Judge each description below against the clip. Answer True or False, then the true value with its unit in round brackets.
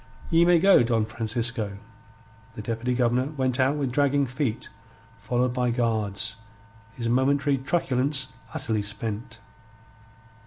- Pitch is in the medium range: False (125 Hz)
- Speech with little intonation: False (3.1 semitones)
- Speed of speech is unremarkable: False (120 wpm)